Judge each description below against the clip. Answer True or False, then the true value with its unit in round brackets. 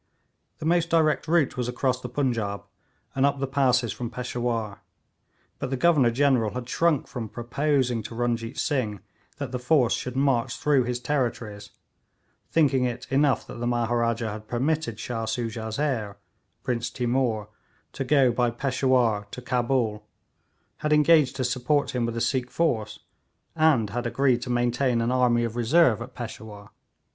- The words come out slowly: False (160 wpm)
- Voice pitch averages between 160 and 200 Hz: False (125 Hz)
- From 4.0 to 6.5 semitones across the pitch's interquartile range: False (2.7 semitones)